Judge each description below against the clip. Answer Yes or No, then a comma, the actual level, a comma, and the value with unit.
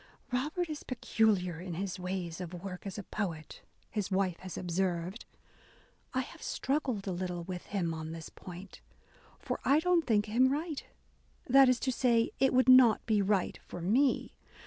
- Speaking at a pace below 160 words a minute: No, average, 170 wpm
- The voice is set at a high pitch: Yes, high, 200 Hz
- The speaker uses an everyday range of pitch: No, wide, 6.1 semitones